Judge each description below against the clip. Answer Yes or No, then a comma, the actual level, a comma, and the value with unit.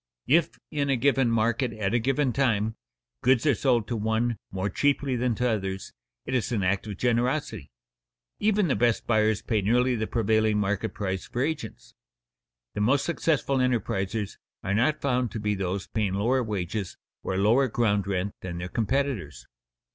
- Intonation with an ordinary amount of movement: Yes, average, 4.0 semitones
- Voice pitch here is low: Yes, low, 115 Hz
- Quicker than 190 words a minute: No, average, 170 wpm